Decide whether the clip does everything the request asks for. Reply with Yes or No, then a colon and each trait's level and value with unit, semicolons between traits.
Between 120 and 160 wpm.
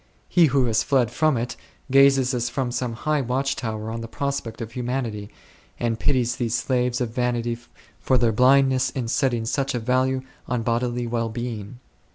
No: average, 180 wpm